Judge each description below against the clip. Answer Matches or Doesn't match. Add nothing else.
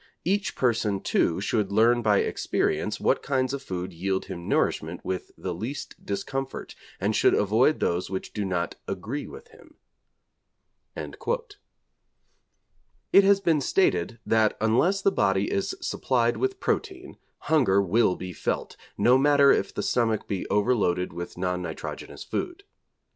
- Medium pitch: Doesn't match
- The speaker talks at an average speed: Matches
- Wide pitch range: Matches